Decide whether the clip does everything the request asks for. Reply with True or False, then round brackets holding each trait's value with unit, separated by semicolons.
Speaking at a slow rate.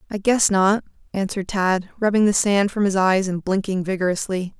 False (185 wpm)